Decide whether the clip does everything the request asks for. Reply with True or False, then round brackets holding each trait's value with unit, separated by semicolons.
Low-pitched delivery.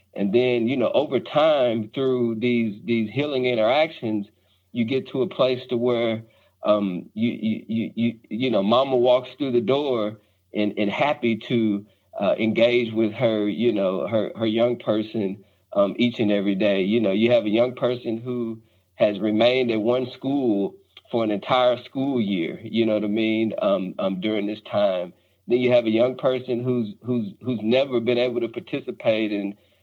True (115 Hz)